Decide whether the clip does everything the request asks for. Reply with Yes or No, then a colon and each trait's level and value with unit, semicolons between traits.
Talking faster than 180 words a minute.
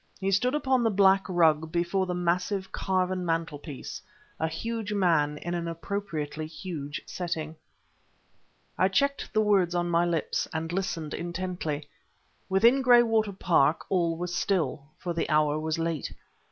No: average, 145 wpm